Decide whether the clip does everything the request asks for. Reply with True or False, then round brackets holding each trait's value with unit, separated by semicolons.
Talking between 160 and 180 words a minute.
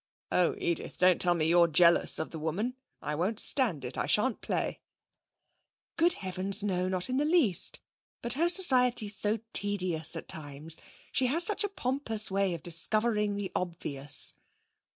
True (165 wpm)